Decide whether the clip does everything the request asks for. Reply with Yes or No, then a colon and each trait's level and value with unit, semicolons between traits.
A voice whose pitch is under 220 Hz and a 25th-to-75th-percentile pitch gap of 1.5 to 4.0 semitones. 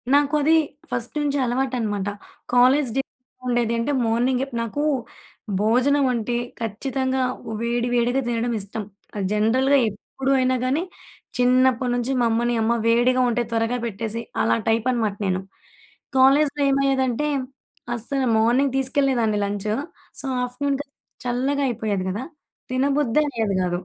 No: high, 245 Hz; average, 2.9 semitones